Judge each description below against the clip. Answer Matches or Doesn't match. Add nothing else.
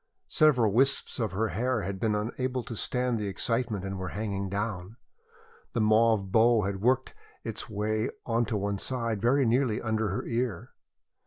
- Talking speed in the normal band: Matches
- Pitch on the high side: Doesn't match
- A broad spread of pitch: Doesn't match